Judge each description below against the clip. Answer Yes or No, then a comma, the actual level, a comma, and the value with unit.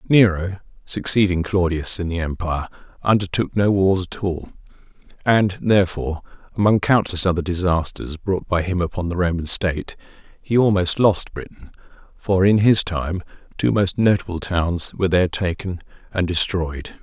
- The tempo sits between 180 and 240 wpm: No, average, 145 wpm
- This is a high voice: No, very low, 90 Hz